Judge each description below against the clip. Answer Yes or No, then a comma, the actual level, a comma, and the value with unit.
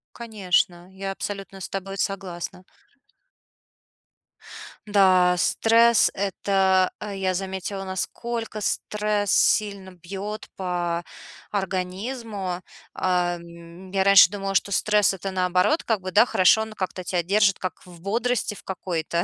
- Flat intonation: Yes, narrow, 2.1 semitones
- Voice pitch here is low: No, high, 195 Hz